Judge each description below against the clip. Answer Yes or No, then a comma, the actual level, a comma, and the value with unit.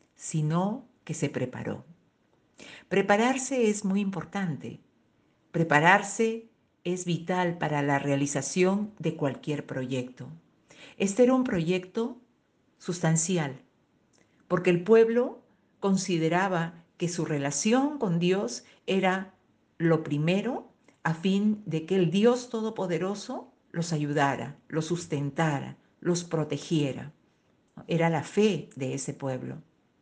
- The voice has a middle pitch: Yes, medium, 175 Hz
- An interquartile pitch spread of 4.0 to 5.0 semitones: Yes, average, 4.5 semitones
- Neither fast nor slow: No, slow, 105 wpm